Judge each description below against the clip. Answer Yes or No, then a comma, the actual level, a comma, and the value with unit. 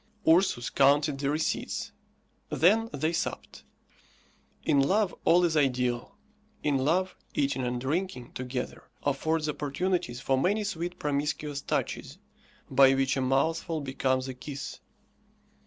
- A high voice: No, medium, 145 Hz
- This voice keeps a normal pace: No, slow, 125 wpm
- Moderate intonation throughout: Yes, average, 3.6 semitones